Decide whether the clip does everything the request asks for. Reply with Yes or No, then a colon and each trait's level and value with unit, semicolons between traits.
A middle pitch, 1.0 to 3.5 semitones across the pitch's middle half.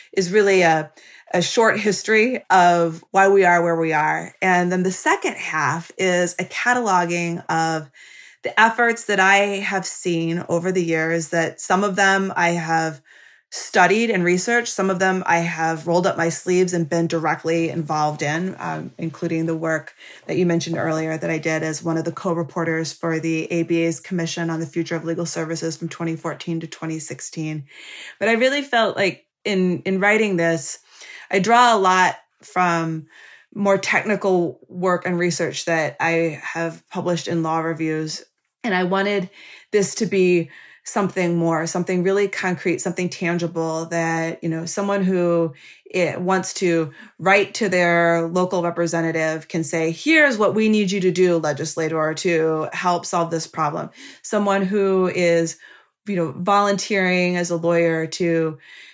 Yes: medium, 175 Hz; narrow, 2.6 semitones